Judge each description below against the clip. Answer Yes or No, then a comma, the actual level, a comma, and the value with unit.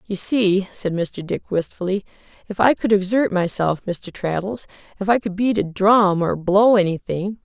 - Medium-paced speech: Yes, average, 160 wpm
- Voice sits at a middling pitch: No, high, 195 Hz